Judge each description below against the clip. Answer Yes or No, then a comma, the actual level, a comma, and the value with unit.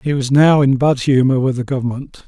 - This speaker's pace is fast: Yes, fast, 235 wpm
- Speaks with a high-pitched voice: No, low, 135 Hz